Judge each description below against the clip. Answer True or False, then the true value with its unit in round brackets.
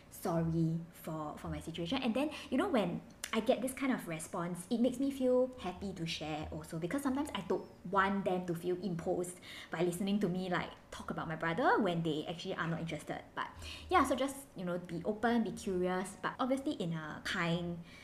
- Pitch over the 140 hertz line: True (185 Hz)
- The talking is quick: True (210 wpm)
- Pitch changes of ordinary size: False (6.0 semitones)